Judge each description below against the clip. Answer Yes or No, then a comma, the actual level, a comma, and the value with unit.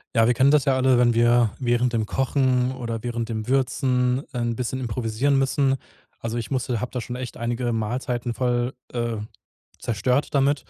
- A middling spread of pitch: No, narrow, 1.9 semitones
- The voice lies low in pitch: Yes, low, 125 Hz